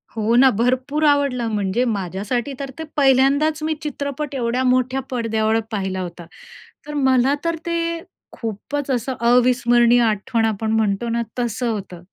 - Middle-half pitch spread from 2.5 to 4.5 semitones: Yes, average, 3.7 semitones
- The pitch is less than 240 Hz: No, high, 245 Hz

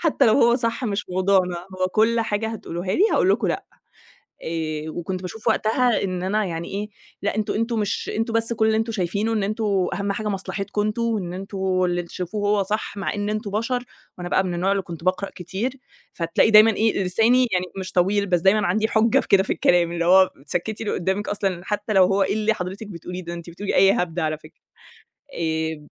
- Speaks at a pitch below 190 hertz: No, high, 195 Hz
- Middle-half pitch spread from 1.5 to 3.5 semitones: Yes, average, 3.2 semitones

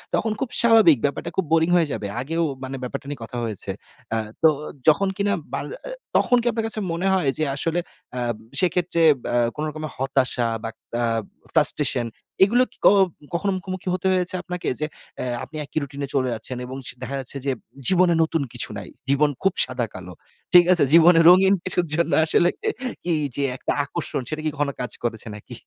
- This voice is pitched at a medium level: Yes, medium, 160 Hz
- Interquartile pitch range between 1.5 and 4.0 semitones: No, average, 5.2 semitones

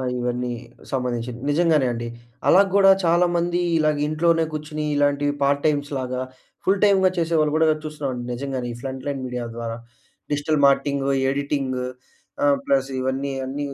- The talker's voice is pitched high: No, medium, 140 Hz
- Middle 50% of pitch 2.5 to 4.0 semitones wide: Yes, average, 3.1 semitones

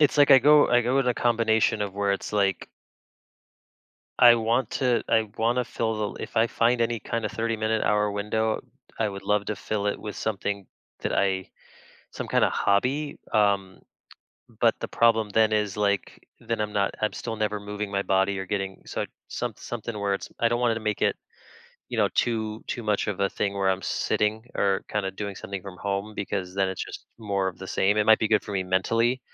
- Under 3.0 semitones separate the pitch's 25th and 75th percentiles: Yes, narrow, 2.5 semitones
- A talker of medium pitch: No, low, 105 Hz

